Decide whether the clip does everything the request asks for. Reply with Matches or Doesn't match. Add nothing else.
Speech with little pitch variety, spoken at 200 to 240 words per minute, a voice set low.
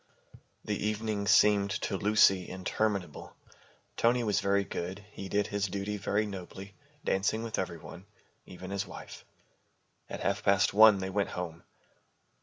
Doesn't match